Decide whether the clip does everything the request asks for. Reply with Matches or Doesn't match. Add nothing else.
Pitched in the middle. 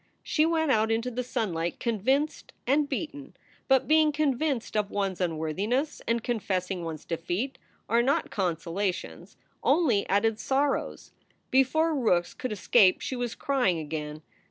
Doesn't match